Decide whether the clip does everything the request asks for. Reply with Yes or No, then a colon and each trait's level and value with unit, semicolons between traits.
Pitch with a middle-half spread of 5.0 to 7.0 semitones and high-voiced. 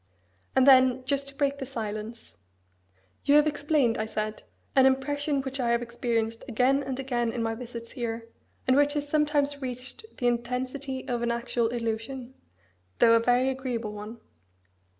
No: average, 2.8 semitones; very high, 255 Hz